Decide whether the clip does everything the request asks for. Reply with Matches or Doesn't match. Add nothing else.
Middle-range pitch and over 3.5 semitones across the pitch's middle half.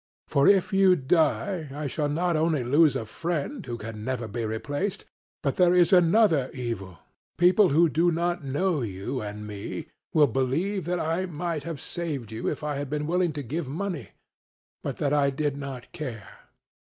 Matches